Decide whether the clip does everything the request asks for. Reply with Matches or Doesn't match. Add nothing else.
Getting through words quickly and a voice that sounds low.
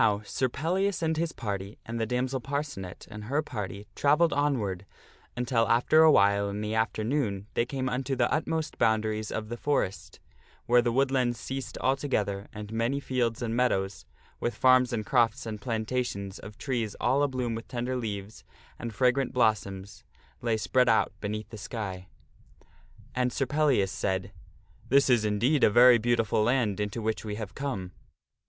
Doesn't match